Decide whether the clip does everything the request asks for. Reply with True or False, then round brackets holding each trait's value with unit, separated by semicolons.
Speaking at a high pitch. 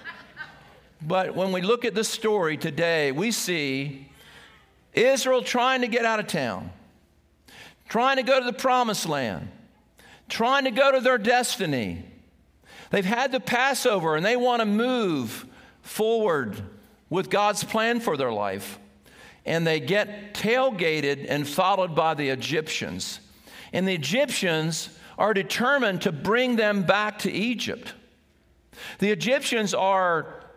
True (205 Hz)